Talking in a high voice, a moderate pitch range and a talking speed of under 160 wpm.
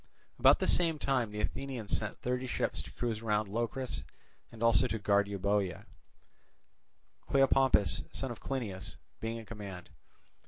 No: low, 115 Hz; average, 3.8 semitones; average, 145 wpm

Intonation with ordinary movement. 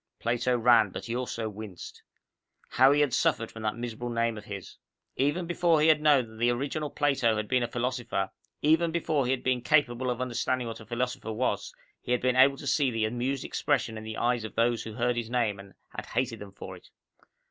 Yes: average, 3.1 semitones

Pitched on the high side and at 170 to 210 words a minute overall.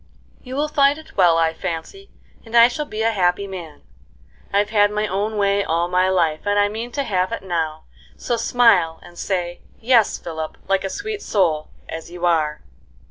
Yes: high, 195 Hz; average, 190 wpm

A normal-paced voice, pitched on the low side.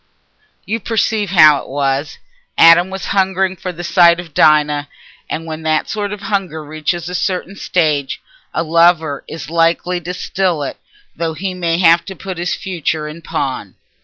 No: average, 170 wpm; medium, 170 Hz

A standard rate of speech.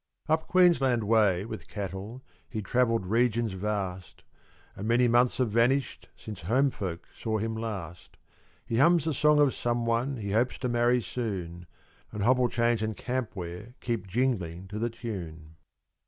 Yes: average, 155 wpm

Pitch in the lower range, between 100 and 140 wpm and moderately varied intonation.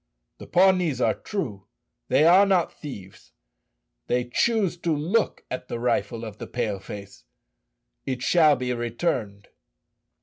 No: low, 125 Hz; slow, 135 wpm; wide, 7.4 semitones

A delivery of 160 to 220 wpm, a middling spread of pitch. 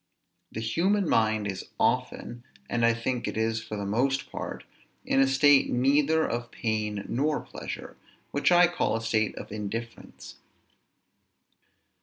No: average, 145 wpm; average, 4.1 semitones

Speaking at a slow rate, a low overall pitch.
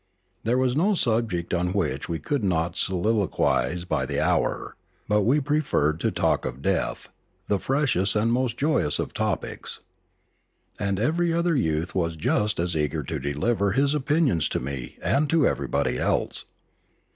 No: average, 155 wpm; low, 100 Hz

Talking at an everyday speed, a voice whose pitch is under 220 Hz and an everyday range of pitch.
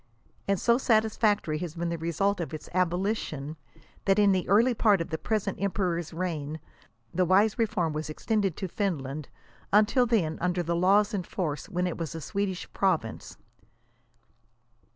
Yes: average, 165 wpm; medium, 185 Hz; average, 3.8 semitones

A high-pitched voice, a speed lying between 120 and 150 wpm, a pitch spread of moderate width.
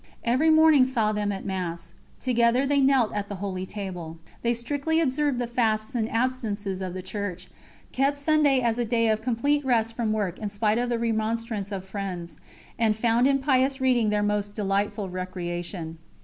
No: high, 225 Hz; average, 180 wpm; average, 4.2 semitones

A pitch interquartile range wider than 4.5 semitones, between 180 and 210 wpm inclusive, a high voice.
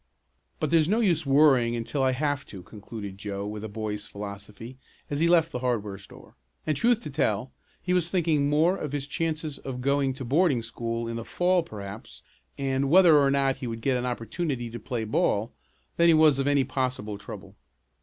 No: average, 5.2 semitones; average, 200 wpm; low, 135 Hz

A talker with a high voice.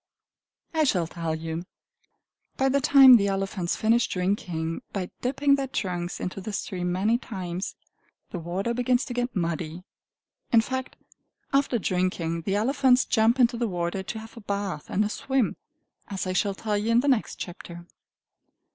Yes: high, 205 Hz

